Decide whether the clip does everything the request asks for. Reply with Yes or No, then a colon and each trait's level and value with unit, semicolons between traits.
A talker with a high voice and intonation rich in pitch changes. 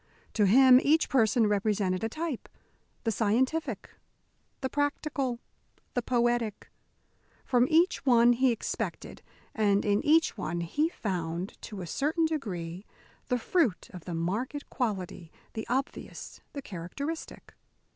Yes: high, 235 Hz; wide, 5.7 semitones